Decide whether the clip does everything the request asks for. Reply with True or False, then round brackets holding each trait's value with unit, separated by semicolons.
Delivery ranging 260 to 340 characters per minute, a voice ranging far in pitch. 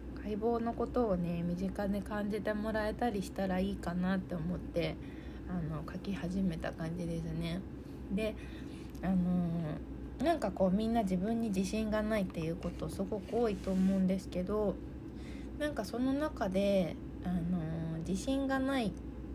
False (300 characters per minute; 3.8 semitones)